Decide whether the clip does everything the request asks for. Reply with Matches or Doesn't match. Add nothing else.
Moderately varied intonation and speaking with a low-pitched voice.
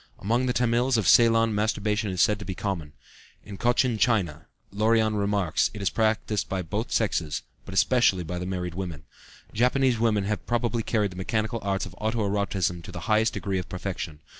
Matches